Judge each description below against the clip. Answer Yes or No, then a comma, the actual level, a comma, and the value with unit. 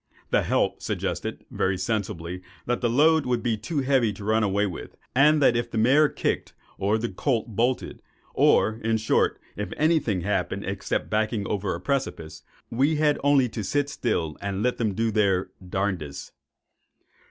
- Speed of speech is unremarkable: Yes, average, 170 wpm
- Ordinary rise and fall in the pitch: Yes, average, 5.0 semitones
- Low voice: Yes, low, 110 Hz